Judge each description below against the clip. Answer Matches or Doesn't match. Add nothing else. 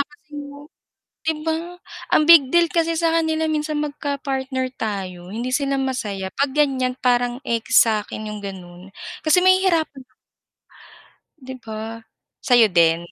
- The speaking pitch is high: Matches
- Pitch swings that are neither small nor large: Doesn't match